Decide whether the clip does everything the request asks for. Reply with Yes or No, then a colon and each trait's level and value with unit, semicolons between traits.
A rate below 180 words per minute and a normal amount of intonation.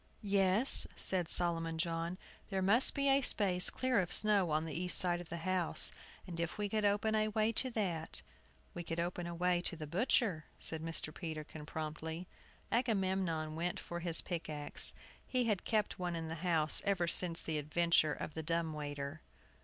No: average, 190 wpm; average, 3.5 semitones